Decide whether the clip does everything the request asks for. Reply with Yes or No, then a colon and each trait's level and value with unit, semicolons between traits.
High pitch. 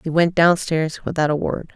No: medium, 165 Hz